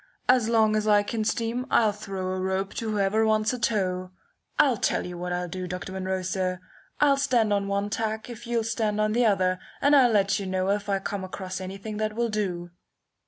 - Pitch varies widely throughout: No, average, 2.8 semitones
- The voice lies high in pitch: Yes, high, 205 Hz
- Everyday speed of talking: No, fast, 215 wpm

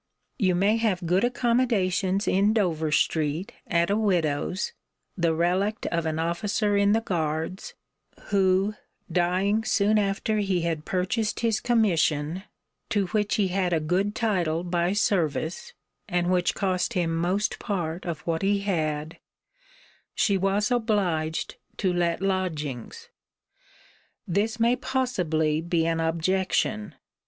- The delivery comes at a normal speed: No, slow, 130 wpm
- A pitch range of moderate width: Yes, average, 3.7 semitones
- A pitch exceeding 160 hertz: Yes, medium, 185 Hz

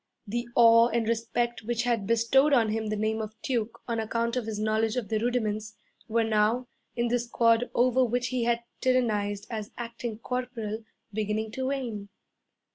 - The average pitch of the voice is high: Yes, high, 230 Hz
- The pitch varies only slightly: Yes, narrow, 1.9 semitones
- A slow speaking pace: No, average, 175 wpm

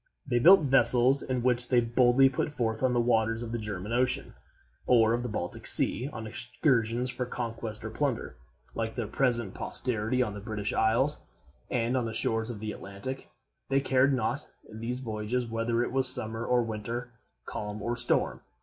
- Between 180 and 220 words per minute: Yes, average, 185 wpm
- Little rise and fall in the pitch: Yes, narrow, 2.2 semitones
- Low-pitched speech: Yes, low, 120 Hz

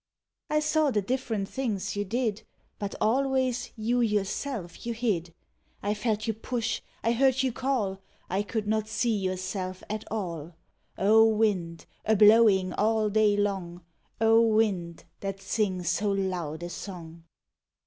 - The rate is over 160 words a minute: No, average, 150 wpm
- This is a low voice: No, high, 210 Hz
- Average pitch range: Yes, average, 3.2 semitones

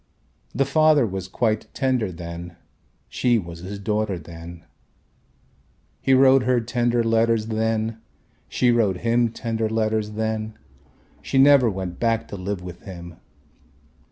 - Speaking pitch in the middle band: No, low, 110 Hz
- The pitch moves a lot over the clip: No, average, 4.0 semitones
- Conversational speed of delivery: No, slow, 130 wpm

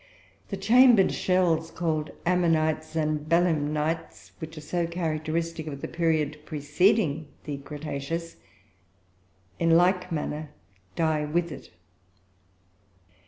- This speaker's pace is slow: Yes, slow, 105 wpm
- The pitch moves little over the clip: Yes, narrow, 2.1 semitones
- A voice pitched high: No, medium, 160 Hz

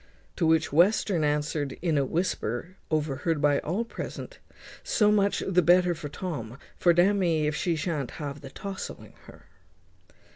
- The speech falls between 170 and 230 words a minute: No, average, 160 wpm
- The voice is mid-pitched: Yes, medium, 165 Hz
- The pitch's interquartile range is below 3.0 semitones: No, average, 3.8 semitones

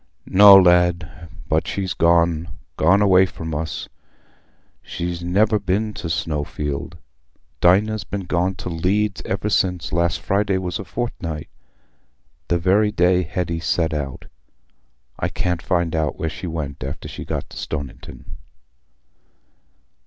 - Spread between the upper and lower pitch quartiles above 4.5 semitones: No, average, 2.8 semitones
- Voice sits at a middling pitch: No, very low, 90 Hz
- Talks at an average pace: No, slow, 130 wpm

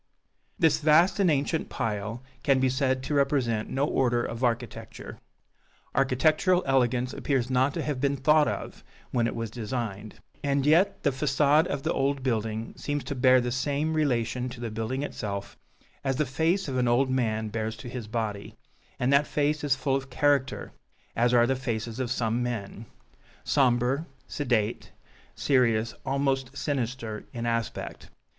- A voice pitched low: Yes, low, 130 Hz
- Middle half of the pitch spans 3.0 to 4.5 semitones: Yes, average, 3.3 semitones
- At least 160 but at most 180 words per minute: Yes, average, 165 wpm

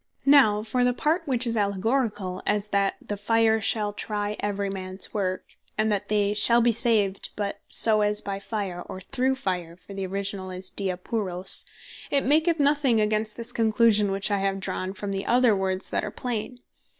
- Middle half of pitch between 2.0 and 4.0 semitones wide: Yes, average, 3.0 semitones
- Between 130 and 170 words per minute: No, average, 185 wpm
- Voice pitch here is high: Yes, high, 210 Hz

